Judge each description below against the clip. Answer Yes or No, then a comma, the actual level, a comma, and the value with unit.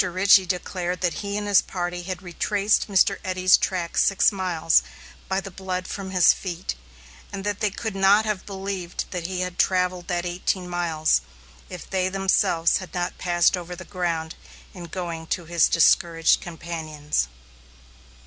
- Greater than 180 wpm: No, average, 160 wpm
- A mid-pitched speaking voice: Yes, medium, 180 Hz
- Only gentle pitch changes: Yes, narrow, 1.9 semitones